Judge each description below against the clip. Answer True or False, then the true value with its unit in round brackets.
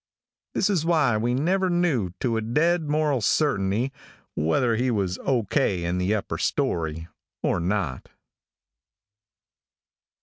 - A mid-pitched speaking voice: False (120 Hz)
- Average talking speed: False (130 wpm)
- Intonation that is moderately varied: False (7.8 semitones)